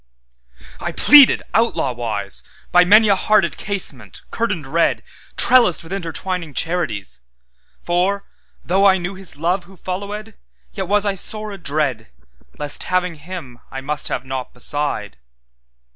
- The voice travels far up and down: Yes, wide, 7.6 semitones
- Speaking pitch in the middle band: Yes, medium, 170 Hz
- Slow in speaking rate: Yes, slow, 115 wpm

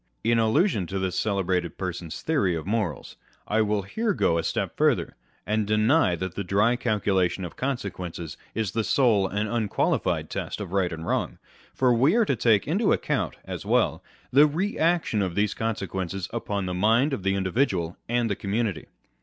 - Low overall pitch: Yes, low, 105 Hz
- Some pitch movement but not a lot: Yes, average, 4.2 semitones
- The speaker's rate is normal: Yes, average, 185 wpm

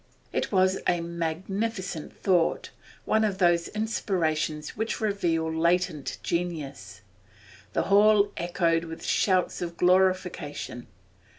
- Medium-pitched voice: Yes, medium, 175 Hz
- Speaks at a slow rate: Yes, slow, 105 wpm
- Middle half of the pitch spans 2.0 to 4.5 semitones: Yes, average, 2.8 semitones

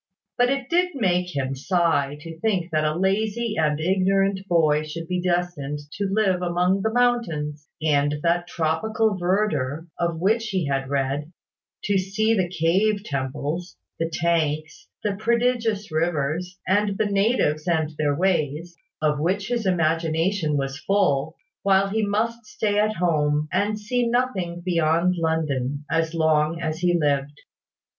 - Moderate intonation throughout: Yes, average, 4.7 semitones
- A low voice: No, medium, 175 Hz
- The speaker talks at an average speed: Yes, average, 150 wpm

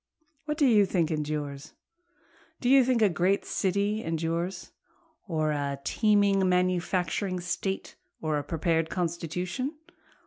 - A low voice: No, medium, 180 Hz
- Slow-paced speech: Yes, slow, 125 wpm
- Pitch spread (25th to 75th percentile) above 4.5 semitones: No, average, 3.7 semitones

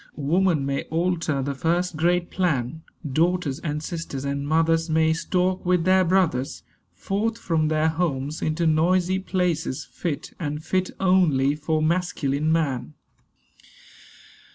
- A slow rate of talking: Yes, slow, 130 wpm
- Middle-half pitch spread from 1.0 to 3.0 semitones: No, average, 3.4 semitones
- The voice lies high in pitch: No, medium, 160 Hz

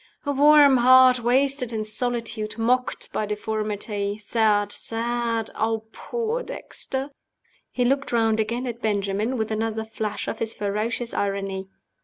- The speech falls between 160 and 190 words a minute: No, slow, 135 wpm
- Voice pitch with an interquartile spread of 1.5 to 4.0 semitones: Yes, average, 2.8 semitones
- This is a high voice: Yes, high, 225 Hz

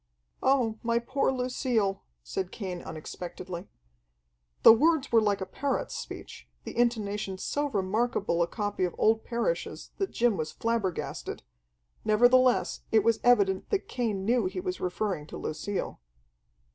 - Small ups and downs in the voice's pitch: No, average, 4.4 semitones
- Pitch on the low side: No, high, 215 Hz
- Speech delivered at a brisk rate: No, average, 140 wpm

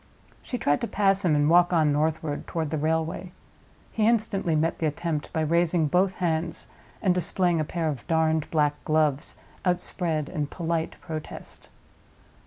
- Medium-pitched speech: Yes, medium, 160 Hz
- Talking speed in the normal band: Yes, average, 160 wpm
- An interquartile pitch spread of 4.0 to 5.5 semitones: No, narrow, 2.4 semitones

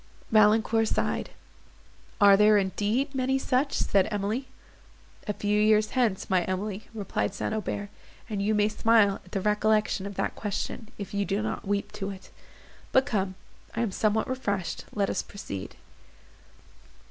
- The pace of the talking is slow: No, average, 150 wpm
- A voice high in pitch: Yes, high, 210 Hz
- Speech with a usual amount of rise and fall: No, narrow, 1.6 semitones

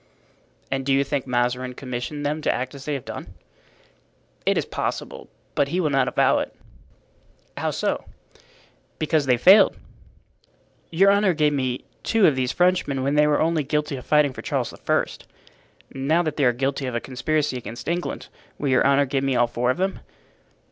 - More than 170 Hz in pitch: No, medium, 140 Hz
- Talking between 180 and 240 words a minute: Yes, average, 185 wpm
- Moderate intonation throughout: Yes, average, 3.2 semitones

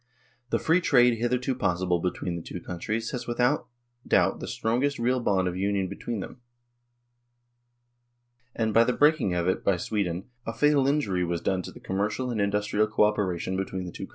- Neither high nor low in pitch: No, low, 105 Hz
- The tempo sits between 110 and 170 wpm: No, average, 185 wpm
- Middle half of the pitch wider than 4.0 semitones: Yes, average, 4.9 semitones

